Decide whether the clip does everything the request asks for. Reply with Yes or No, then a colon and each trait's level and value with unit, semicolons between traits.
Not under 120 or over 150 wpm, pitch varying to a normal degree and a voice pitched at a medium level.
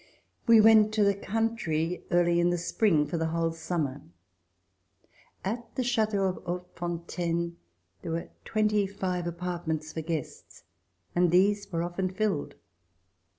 Yes: slow, 135 wpm; average, 3.5 semitones; medium, 175 Hz